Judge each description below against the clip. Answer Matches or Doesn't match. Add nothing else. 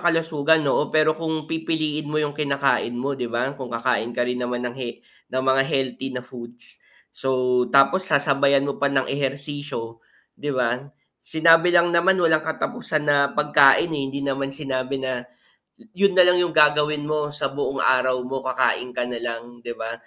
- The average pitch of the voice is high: Doesn't match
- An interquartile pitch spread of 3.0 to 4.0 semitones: Matches